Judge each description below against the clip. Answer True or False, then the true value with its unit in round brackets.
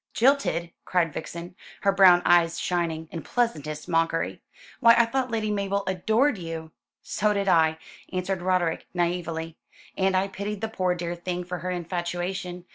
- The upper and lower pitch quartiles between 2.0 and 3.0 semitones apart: True (2.7 semitones)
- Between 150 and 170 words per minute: True (160 wpm)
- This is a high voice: False (180 Hz)